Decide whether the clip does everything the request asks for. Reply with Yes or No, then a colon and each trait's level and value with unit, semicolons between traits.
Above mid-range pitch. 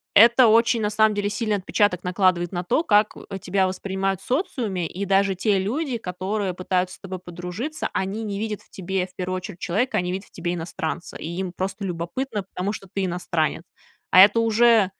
Yes: high, 195 Hz